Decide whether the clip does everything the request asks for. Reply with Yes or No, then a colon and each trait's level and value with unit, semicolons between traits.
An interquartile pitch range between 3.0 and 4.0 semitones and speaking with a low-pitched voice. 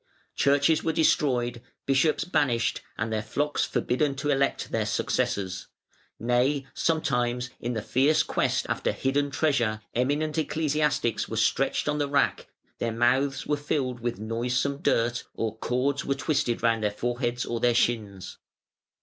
Yes: average, 3.4 semitones; low, 130 Hz